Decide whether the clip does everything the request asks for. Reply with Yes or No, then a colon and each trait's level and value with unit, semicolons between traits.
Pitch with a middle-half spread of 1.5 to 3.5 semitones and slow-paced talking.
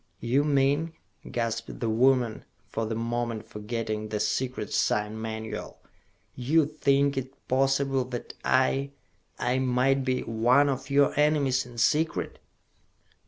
Yes: average, 3.1 semitones; slow, 125 wpm